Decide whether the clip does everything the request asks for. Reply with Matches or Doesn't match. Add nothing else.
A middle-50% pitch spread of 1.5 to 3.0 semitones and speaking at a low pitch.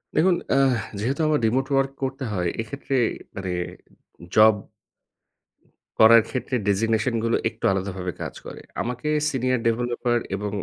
Doesn't match